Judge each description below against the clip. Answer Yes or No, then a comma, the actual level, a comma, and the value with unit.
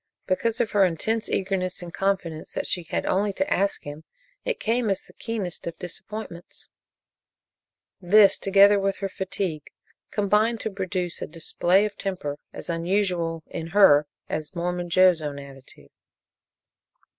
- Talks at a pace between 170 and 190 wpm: No, average, 145 wpm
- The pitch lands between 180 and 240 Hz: Yes, medium, 185 Hz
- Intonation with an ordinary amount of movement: Yes, average, 3.2 semitones